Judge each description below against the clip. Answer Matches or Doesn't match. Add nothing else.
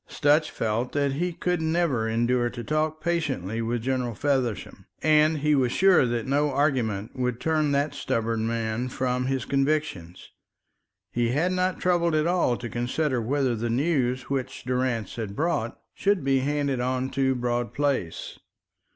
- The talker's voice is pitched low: Matches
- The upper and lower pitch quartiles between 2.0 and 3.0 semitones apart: Doesn't match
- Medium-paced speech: Matches